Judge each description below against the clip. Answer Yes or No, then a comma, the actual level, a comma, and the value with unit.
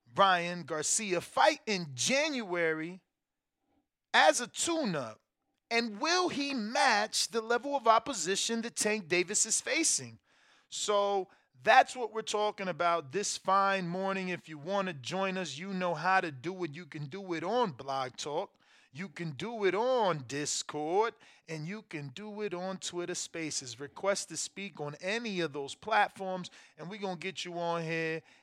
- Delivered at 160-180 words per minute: Yes, average, 165 wpm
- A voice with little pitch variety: No, average, 4.6 semitones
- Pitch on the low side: No, high, 190 Hz